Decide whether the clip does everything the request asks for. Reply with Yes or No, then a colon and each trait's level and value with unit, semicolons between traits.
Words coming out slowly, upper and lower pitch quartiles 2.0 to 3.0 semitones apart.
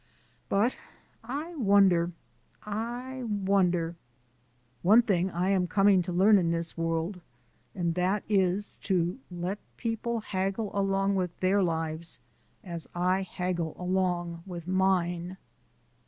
Yes: slow, 120 wpm; narrow, 2.6 semitones